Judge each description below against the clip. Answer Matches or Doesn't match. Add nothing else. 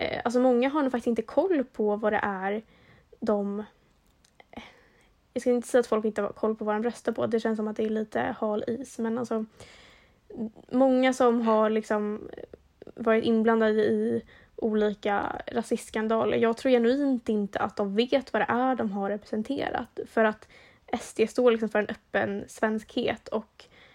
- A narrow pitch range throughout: Matches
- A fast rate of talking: Doesn't match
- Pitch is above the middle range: Matches